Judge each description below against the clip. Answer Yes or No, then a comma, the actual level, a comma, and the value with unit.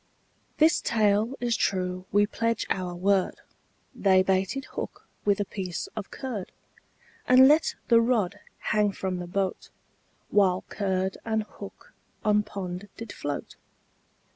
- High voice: Yes, high, 200 Hz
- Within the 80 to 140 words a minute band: Yes, slow, 135 wpm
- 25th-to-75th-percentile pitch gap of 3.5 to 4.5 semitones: No, average, 3.0 semitones